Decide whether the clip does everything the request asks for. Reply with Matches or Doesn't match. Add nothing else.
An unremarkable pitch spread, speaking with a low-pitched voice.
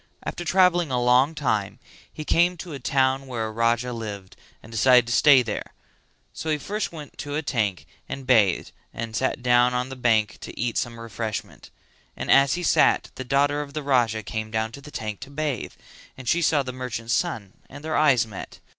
Matches